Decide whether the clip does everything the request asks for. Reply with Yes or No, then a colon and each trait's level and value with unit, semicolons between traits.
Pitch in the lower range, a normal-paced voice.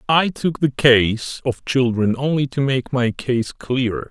Yes: low, 130 Hz; average, 175 wpm